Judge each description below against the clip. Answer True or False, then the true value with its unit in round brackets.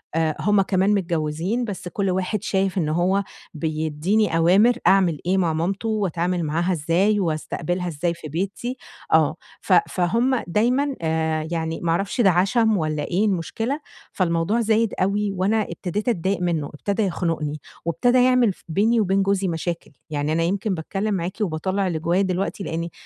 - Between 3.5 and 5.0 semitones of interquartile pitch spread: True (3.8 semitones)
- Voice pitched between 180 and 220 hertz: True (185 Hz)